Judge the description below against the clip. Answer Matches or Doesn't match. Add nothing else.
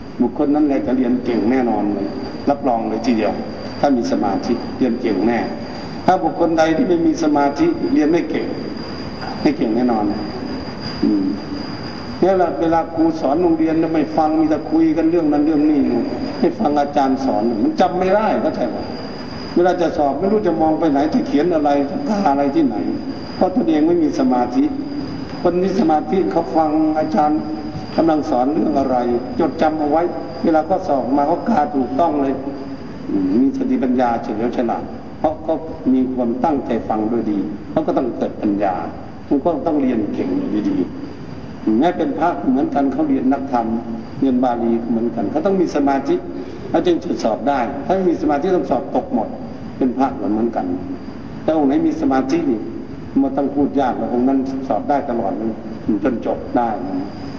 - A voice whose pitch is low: Doesn't match